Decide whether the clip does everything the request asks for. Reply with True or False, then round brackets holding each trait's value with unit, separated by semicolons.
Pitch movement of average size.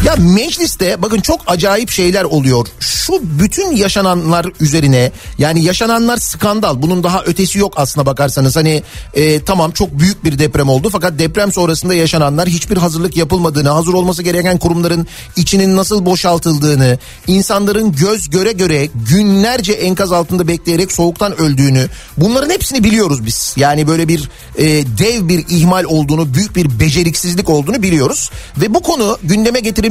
True (4.2 semitones)